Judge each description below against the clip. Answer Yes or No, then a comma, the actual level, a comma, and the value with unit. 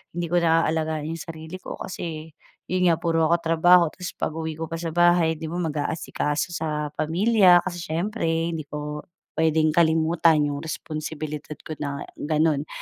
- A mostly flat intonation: Yes, narrow, 1.7 semitones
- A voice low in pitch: No, medium, 160 Hz